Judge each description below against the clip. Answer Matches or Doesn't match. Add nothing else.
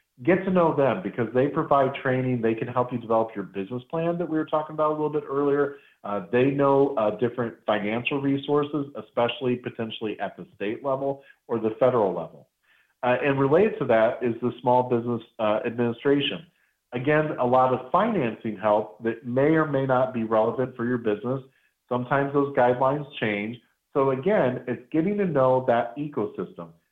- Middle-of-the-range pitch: Doesn't match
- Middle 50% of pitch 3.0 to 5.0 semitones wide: Matches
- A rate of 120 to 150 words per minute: Doesn't match